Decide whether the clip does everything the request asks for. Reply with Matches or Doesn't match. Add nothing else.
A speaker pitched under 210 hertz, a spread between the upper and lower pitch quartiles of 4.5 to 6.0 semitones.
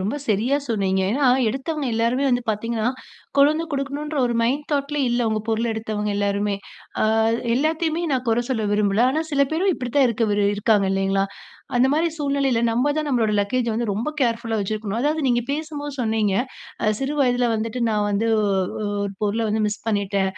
Doesn't match